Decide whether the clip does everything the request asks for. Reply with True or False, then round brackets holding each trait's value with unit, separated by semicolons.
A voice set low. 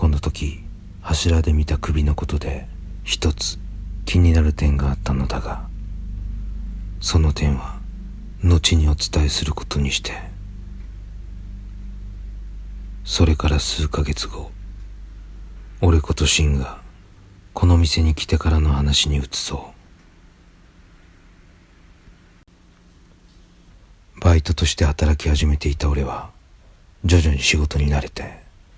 True (85 Hz)